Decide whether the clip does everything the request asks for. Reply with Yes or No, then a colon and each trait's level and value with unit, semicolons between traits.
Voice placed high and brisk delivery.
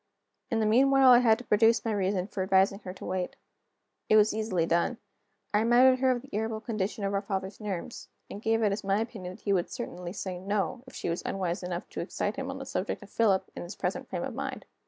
Yes: high, 210 Hz; fast, 240 wpm